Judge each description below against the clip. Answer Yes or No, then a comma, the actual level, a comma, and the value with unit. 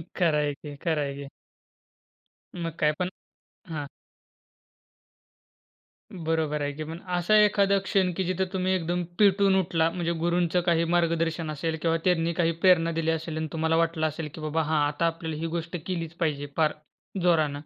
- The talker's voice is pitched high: No, medium, 165 Hz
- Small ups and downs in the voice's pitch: Yes, narrow, 2.0 semitones